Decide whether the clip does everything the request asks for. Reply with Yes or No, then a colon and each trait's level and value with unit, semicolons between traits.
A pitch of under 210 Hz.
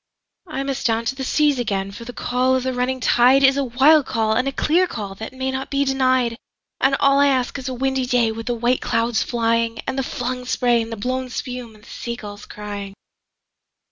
No: very high, 250 Hz